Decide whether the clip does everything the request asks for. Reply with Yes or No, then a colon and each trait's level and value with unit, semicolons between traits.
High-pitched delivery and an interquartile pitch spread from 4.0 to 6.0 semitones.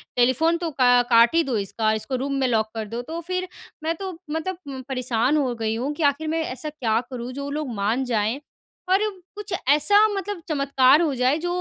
Yes: very high, 275 Hz; average, 5.0 semitones